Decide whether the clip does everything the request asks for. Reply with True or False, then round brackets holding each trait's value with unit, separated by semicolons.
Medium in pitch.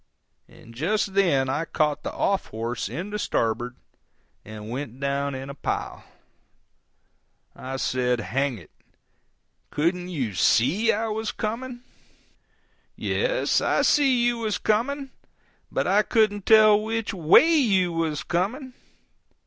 True (180 Hz)